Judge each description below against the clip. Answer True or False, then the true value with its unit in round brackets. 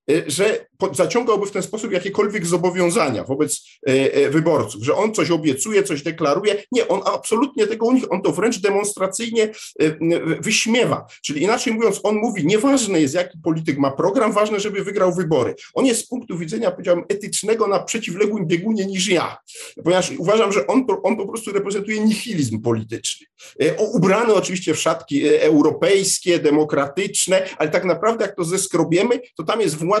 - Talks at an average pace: False (170 wpm)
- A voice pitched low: False (190 Hz)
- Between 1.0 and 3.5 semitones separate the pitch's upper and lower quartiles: False (4.5 semitones)